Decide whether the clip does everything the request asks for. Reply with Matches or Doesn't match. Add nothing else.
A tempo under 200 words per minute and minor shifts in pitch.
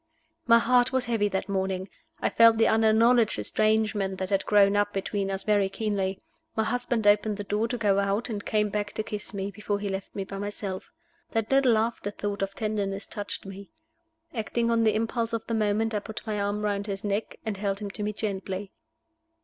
Doesn't match